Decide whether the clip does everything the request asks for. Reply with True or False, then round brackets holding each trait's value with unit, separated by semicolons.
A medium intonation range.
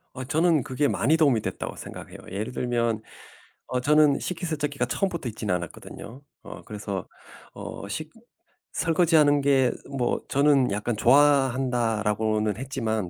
True (5.0 semitones)